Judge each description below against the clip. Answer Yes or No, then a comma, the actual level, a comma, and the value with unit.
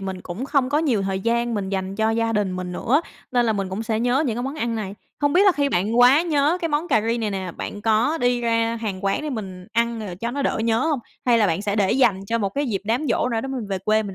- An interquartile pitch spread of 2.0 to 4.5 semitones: Yes, average, 4.2 semitones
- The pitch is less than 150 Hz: No, high, 230 Hz